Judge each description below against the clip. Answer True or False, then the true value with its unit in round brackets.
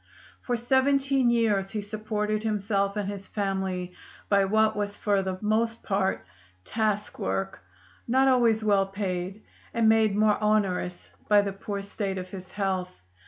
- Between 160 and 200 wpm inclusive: False (150 wpm)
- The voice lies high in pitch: True (205 Hz)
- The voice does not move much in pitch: True (2.1 semitones)